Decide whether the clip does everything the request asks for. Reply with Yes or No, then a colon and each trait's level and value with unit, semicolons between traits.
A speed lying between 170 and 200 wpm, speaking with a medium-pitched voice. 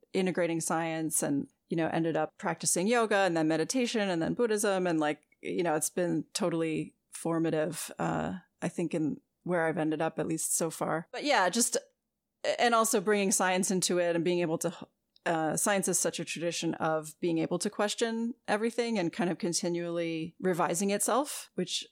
Yes: average, 185 wpm; medium, 175 Hz